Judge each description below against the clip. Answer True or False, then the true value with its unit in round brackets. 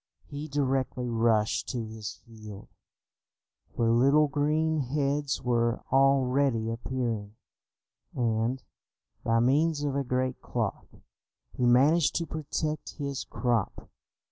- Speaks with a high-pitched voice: False (130 Hz)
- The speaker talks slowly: True (110 wpm)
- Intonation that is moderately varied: True (3.7 semitones)